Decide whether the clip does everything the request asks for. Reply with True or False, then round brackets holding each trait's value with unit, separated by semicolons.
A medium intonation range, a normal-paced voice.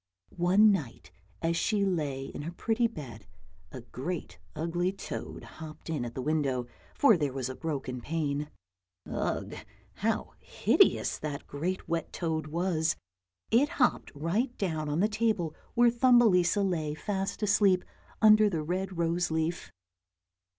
True (4.7 semitones; 145 wpm)